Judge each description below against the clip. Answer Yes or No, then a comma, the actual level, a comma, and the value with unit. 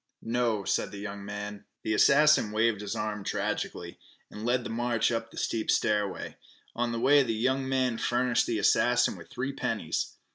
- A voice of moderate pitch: No, low, 115 Hz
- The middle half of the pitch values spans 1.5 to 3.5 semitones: Yes, average, 2.8 semitones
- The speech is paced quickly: No, average, 180 wpm